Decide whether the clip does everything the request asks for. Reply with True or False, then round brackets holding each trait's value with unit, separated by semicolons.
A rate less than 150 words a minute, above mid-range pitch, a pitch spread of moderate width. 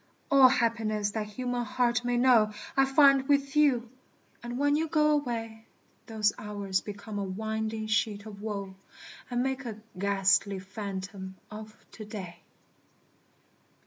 True (140 wpm; 220 Hz; 3.5 semitones)